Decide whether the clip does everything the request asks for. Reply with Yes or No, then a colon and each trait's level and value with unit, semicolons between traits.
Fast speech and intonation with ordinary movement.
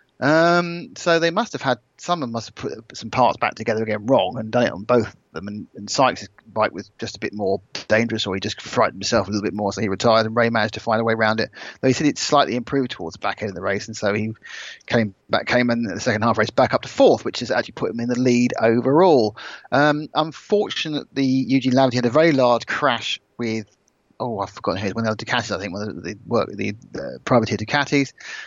Yes: fast, 255 wpm; average, 3.8 semitones